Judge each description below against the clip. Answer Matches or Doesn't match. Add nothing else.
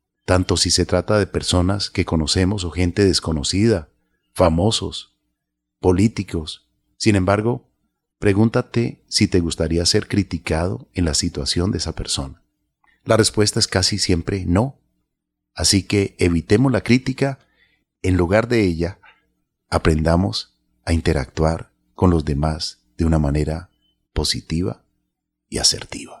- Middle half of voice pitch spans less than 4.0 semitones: Doesn't match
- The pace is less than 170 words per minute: Matches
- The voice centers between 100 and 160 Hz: Doesn't match